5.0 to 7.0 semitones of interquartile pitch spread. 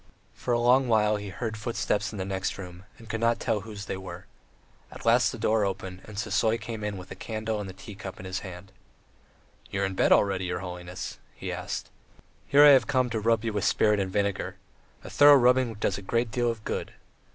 No: average, 3.2 semitones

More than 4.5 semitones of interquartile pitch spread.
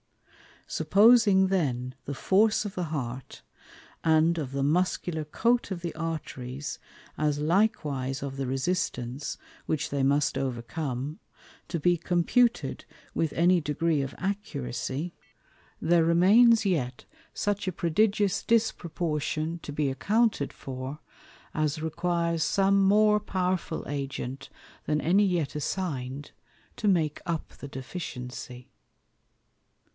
Yes: average, 5.1 semitones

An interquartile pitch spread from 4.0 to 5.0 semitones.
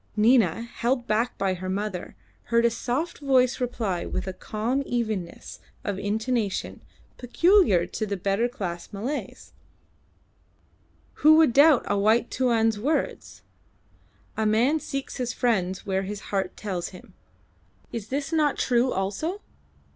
Yes: average, 4.5 semitones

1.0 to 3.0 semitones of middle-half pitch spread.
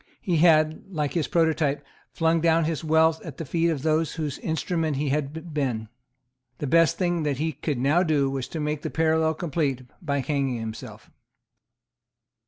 Yes: narrow, 2.6 semitones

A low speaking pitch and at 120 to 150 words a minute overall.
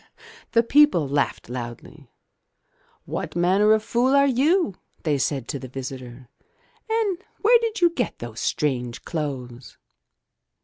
No: medium, 160 Hz; average, 140 wpm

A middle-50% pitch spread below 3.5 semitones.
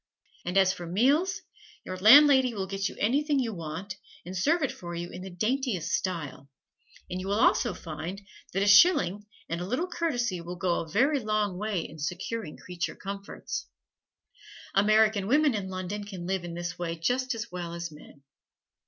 No: average, 4.9 semitones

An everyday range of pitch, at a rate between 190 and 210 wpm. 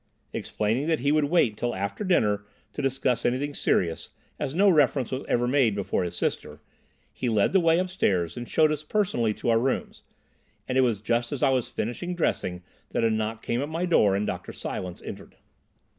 No: wide, 6.0 semitones; average, 200 wpm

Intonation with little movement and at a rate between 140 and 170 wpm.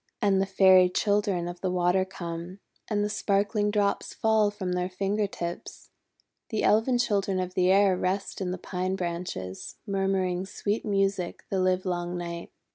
Yes: narrow, 2.1 semitones; average, 160 wpm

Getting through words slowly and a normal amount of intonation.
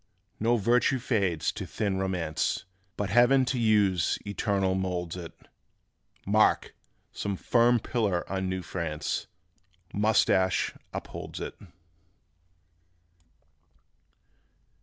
Yes: slow, 95 wpm; average, 3.8 semitones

